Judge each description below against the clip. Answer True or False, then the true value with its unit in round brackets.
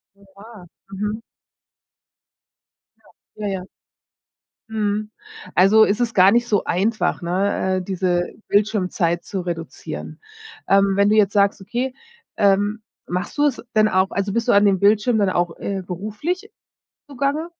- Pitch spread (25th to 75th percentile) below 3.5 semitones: True (2.5 semitones)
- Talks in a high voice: True (200 Hz)